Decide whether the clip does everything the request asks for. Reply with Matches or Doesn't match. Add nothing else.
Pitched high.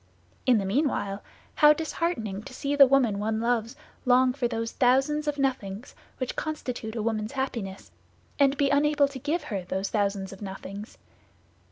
Matches